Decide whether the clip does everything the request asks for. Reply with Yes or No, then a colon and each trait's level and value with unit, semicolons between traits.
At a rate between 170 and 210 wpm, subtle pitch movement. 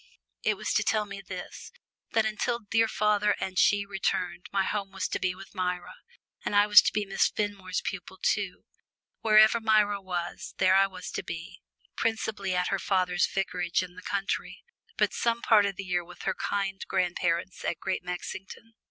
Yes: average, 185 wpm; narrow, 2.1 semitones